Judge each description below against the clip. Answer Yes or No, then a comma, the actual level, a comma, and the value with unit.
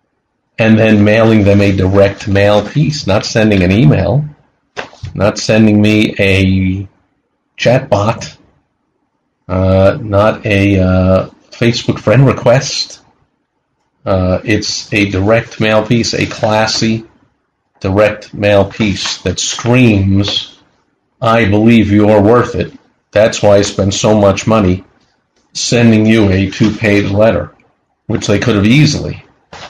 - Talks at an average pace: No, slow, 125 wpm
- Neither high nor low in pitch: No, low, 105 Hz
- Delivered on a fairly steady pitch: Yes, narrow, 2.2 semitones